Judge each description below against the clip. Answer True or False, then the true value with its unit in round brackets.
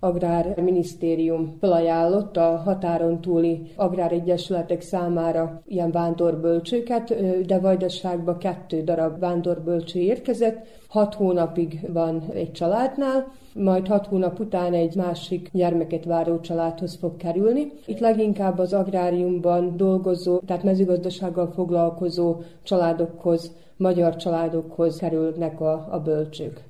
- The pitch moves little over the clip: True (2.0 semitones)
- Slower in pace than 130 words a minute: True (105 wpm)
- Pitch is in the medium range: True (175 Hz)